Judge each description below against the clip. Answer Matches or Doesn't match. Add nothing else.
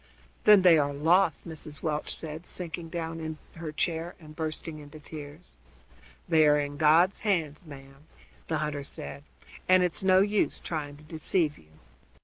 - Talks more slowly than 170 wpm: Matches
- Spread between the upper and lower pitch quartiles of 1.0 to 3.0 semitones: Matches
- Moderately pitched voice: Matches